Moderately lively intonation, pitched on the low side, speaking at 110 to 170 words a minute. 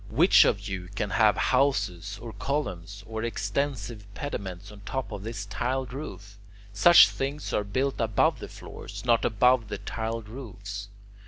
Yes: average, 3.9 semitones; low, 110 Hz; average, 155 wpm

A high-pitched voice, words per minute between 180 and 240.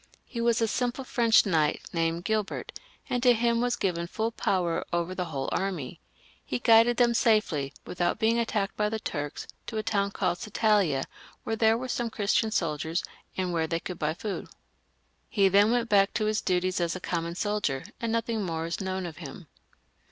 Yes: high, 200 Hz; average, 190 wpm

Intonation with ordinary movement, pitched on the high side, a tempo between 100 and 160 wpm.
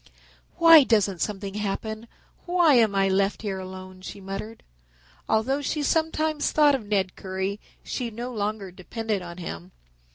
Yes: average, 4.8 semitones; high, 210 Hz; average, 150 wpm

